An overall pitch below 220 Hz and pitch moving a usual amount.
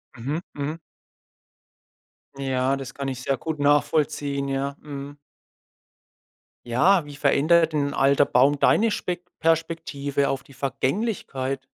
No: medium, 140 Hz; narrow, 2.3 semitones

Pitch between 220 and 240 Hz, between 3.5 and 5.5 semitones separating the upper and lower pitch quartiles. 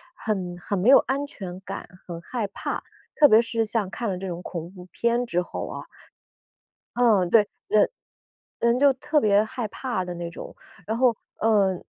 No: high, 210 Hz; average, 4.4 semitones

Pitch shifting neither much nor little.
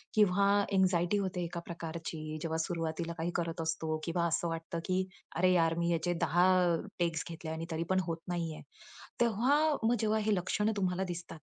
No: narrow, 2.3 semitones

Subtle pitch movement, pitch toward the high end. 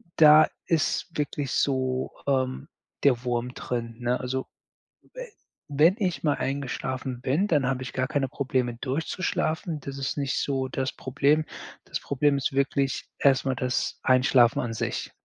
No: narrow, 2.0 semitones; low, 135 Hz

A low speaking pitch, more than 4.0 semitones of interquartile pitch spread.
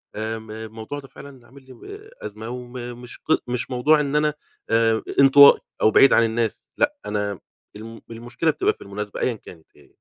No: low, 120 Hz; average, 3.7 semitones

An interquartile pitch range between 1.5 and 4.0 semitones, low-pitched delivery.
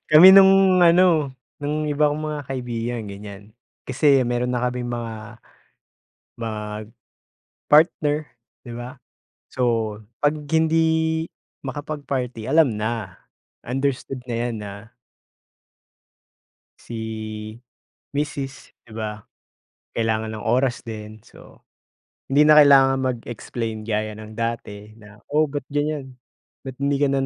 No: average, 4.7 semitones; low, 125 Hz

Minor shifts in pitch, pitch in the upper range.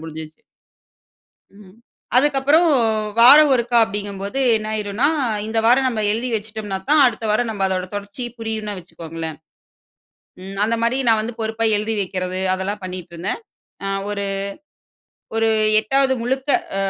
No: average, 3.8 semitones; high, 215 Hz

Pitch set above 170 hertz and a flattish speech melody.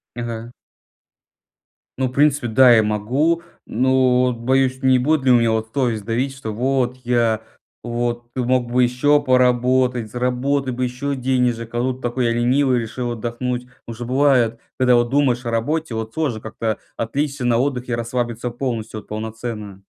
No: low, 125 Hz; narrow, 1.9 semitones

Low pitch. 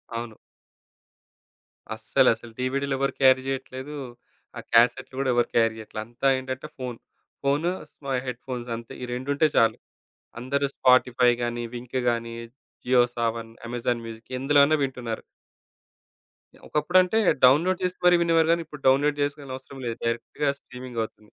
Yes: low, 130 Hz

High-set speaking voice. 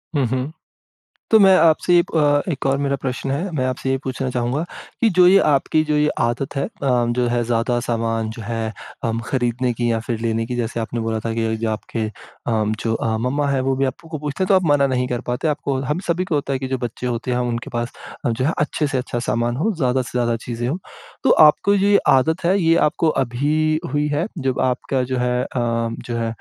No: low, 130 Hz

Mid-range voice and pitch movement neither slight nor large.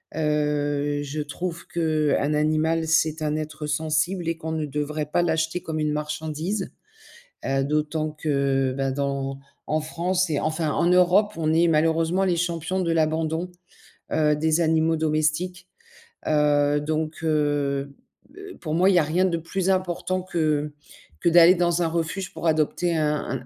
No: medium, 155 Hz; narrow, 2.1 semitones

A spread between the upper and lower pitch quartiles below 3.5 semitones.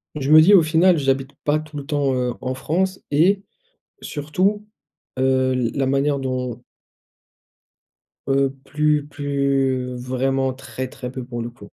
Yes: narrow, 2.6 semitones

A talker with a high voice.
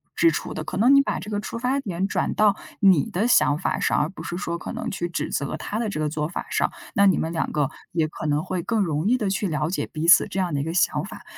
No: medium, 180 Hz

